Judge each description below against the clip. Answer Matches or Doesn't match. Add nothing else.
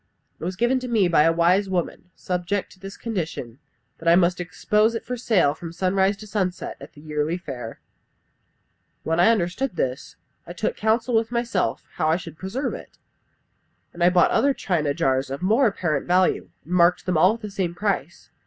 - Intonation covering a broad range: Doesn't match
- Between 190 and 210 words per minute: Matches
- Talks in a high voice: Doesn't match